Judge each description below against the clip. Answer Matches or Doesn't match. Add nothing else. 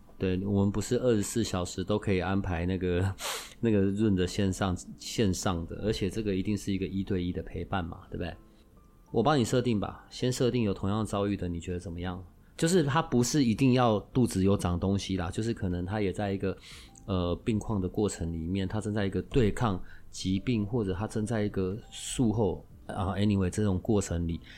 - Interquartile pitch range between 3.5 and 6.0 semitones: Doesn't match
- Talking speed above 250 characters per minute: Matches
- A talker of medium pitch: Doesn't match